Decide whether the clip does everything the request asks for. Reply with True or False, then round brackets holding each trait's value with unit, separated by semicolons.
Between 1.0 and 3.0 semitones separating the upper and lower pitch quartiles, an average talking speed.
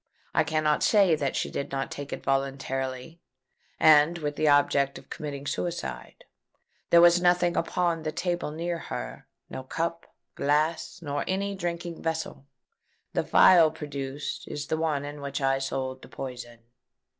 False (3.6 semitones; 150 wpm)